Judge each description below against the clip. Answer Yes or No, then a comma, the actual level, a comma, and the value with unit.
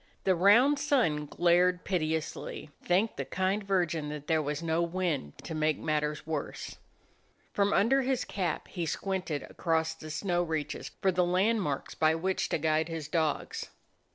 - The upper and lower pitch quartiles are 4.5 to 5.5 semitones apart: No, average, 3.4 semitones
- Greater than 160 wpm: No, average, 155 wpm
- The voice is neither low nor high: Yes, medium, 170 Hz